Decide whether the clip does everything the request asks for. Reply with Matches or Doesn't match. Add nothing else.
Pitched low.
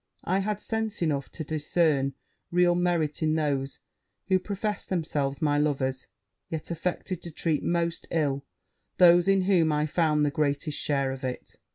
Doesn't match